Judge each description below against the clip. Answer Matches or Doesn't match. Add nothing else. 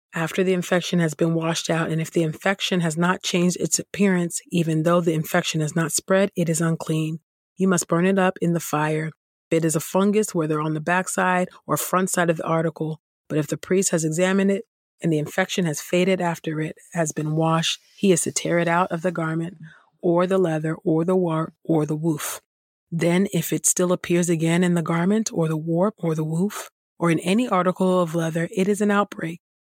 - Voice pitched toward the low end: Doesn't match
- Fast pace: Matches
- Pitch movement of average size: Doesn't match